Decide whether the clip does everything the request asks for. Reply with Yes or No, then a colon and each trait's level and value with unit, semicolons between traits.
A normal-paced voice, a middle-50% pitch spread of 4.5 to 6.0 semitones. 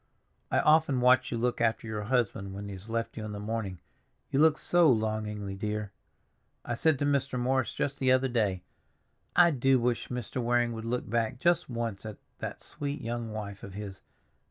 No: average, 195 wpm; average, 3.5 semitones